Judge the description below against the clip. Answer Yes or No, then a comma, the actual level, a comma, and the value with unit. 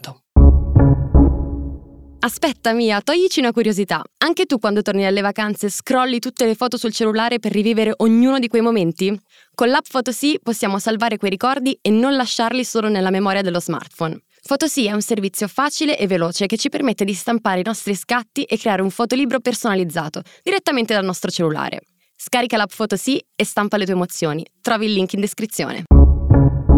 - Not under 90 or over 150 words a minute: No, fast, 170 wpm